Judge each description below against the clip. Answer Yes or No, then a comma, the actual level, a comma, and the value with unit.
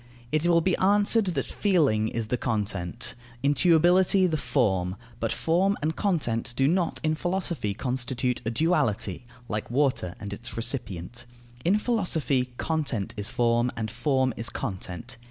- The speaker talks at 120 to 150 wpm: Yes, average, 145 wpm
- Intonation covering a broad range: Yes, wide, 6.9 semitones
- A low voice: Yes, low, 130 Hz